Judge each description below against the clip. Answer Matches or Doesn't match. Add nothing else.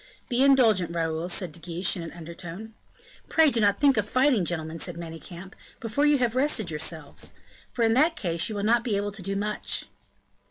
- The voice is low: Doesn't match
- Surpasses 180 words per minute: Matches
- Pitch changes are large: Matches